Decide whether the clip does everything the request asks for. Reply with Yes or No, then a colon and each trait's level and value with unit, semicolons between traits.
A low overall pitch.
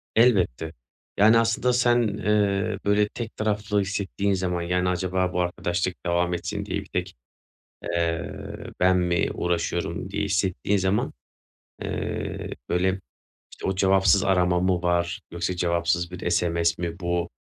Yes: very low, 90 Hz